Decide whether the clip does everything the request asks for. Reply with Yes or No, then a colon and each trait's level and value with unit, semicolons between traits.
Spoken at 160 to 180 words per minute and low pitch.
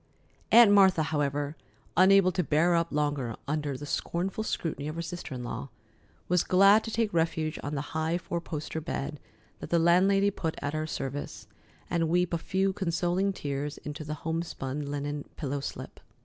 No: average, 175 wpm; medium, 160 Hz